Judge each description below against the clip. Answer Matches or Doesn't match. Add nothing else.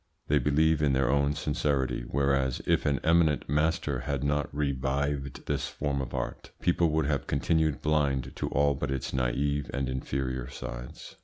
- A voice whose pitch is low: Matches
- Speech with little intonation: Matches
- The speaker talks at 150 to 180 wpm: Matches